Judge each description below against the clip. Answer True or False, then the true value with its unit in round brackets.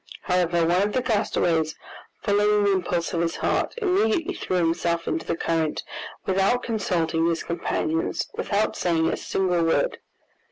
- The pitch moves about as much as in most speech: True (3.8 semitones)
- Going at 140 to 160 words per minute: True (150 wpm)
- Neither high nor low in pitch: True (180 Hz)